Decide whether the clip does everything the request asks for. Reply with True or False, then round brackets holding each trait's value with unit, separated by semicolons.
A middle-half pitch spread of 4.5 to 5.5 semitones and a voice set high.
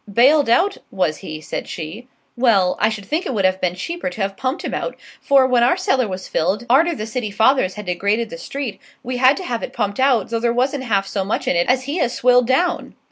True (4.9 semitones; 235 Hz)